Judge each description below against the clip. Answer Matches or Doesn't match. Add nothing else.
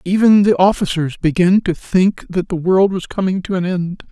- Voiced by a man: Matches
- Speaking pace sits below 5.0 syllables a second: Matches